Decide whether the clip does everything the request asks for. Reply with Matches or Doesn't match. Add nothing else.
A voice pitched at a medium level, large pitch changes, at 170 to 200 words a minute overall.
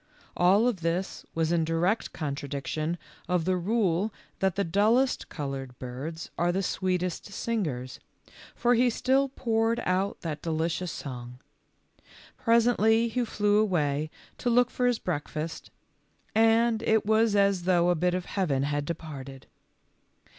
Doesn't match